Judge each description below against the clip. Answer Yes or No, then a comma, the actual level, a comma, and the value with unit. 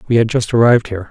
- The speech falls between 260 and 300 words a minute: Yes, fast, 270 wpm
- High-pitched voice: No, low, 115 Hz